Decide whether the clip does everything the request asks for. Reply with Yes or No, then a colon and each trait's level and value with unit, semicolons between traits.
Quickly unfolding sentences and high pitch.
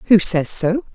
No: average, 190 wpm; high, 200 Hz